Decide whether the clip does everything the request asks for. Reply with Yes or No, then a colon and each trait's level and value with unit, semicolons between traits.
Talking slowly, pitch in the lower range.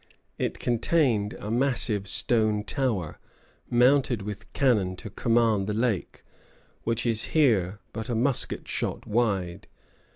Yes: slow, 125 wpm; low, 110 Hz